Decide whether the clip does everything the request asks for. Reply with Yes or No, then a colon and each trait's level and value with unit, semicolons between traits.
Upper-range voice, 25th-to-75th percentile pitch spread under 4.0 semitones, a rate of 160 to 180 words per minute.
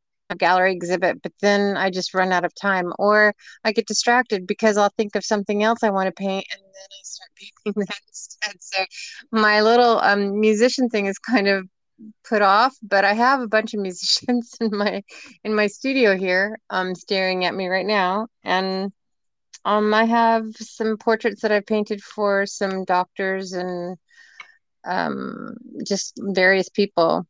Yes: high, 205 Hz; narrow, 2.6 semitones; average, 175 wpm